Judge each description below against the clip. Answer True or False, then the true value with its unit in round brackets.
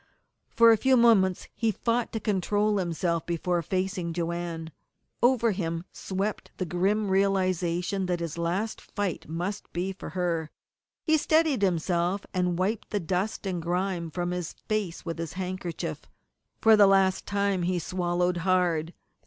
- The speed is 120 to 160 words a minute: True (150 wpm)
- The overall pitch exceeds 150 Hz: True (185 Hz)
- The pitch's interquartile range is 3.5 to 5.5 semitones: False (2.7 semitones)